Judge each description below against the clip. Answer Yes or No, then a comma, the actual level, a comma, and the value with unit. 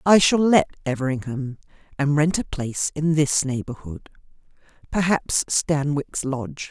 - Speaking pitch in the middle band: Yes, medium, 145 Hz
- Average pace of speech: No, slow, 125 wpm